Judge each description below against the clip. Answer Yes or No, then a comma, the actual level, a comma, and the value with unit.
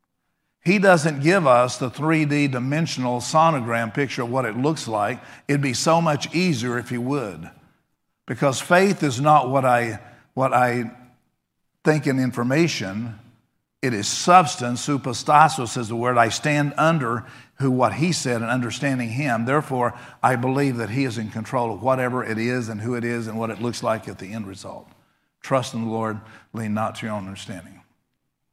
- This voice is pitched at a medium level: No, low, 125 Hz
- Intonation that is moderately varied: Yes, average, 3.6 semitones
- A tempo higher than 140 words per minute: Yes, average, 180 wpm